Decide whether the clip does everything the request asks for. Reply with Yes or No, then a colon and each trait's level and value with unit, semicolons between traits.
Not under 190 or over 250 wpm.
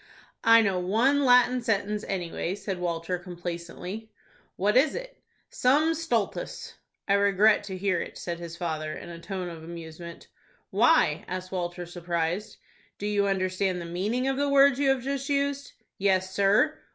No: average, 160 wpm